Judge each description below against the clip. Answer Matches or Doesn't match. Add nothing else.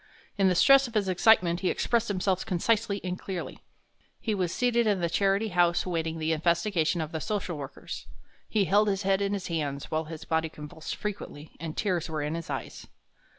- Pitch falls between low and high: Matches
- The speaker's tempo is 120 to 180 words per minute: Doesn't match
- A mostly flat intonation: Doesn't match